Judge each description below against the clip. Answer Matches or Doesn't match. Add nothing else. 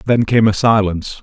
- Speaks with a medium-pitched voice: Doesn't match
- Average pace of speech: Matches